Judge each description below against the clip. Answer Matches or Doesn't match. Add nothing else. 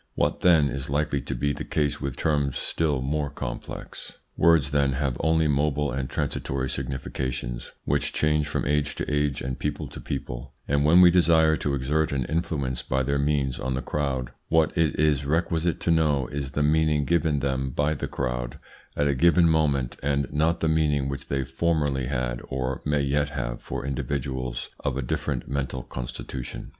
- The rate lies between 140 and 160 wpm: Doesn't match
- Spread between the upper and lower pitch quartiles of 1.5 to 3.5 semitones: Matches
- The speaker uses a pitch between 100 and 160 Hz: Doesn't match